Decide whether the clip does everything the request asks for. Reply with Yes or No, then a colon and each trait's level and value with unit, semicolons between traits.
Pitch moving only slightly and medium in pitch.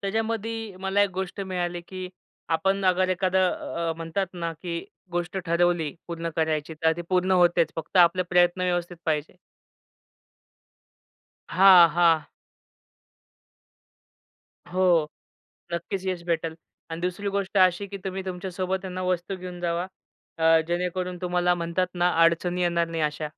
Yes: narrow, 1.8 semitones; medium, 180 Hz